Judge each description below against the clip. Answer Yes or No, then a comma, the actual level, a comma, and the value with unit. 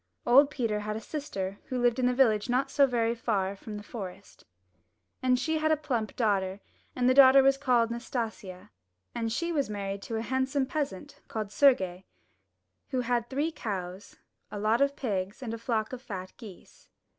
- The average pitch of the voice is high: Yes, high, 235 Hz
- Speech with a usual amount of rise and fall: Yes, average, 4.2 semitones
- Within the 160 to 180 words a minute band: No, average, 190 wpm